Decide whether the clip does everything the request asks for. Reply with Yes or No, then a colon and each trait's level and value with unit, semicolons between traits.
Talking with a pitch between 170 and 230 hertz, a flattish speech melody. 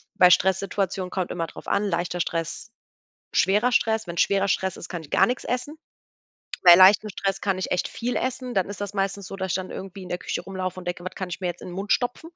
Yes: high, 190 Hz; narrow, 2.2 semitones